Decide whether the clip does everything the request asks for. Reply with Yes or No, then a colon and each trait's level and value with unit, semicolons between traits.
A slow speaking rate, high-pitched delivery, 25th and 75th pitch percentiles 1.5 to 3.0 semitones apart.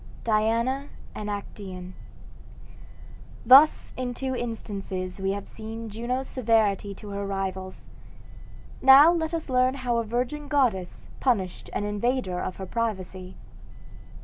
No: slow, 120 wpm; high, 225 Hz; average, 4.7 semitones